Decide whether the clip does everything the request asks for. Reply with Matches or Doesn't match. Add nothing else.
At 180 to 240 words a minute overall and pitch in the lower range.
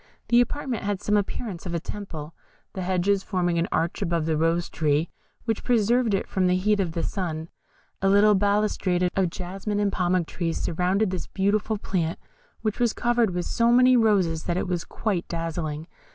Doesn't match